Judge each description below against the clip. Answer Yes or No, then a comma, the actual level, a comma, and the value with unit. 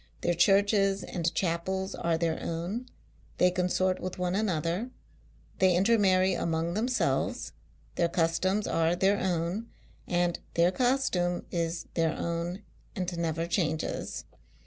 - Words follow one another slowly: Yes, slow, 125 wpm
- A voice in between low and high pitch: Yes, medium, 180 Hz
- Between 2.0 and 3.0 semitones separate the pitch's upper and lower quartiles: Yes, narrow, 2.4 semitones